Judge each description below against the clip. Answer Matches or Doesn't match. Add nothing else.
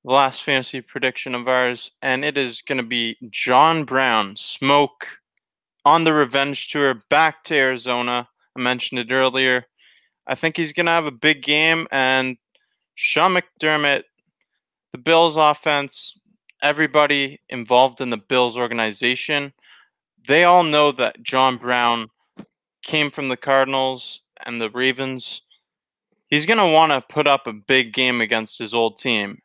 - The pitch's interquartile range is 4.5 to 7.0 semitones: Doesn't match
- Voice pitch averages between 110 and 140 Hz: Matches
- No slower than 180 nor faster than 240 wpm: Doesn't match